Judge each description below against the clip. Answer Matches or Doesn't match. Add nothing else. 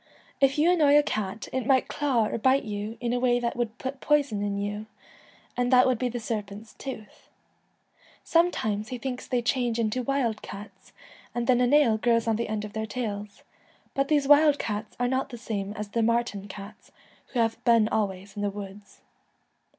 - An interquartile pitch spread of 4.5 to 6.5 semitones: Doesn't match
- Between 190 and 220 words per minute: Matches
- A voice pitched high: Matches